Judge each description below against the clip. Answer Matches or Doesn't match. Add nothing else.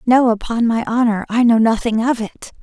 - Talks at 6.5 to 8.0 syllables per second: Doesn't match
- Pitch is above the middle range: Matches